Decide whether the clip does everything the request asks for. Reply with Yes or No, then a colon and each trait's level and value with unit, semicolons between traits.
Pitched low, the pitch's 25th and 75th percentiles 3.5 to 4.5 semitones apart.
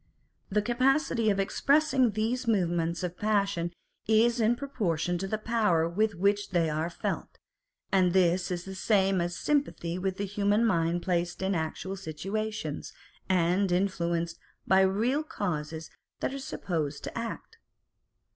No: high, 190 Hz; average, 4.1 semitones